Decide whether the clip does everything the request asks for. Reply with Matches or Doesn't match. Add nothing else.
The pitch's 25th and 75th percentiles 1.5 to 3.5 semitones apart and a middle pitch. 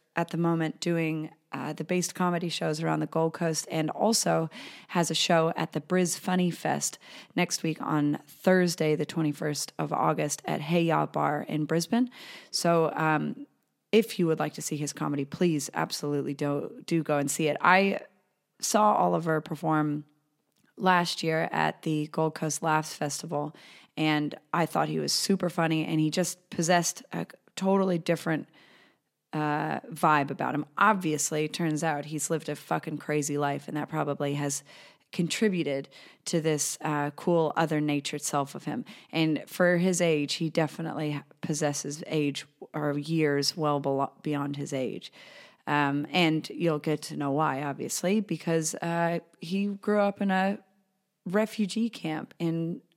Matches